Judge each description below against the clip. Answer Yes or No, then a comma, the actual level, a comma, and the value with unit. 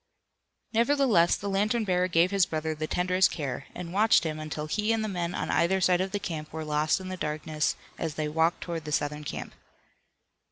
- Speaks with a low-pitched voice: No, medium, 170 Hz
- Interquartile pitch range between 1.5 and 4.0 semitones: Yes, average, 3.7 semitones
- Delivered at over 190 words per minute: Yes, average, 200 wpm